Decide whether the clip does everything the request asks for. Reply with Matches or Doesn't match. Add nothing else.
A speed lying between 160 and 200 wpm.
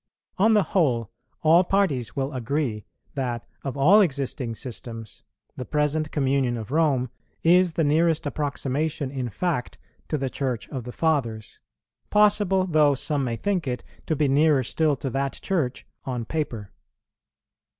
Doesn't match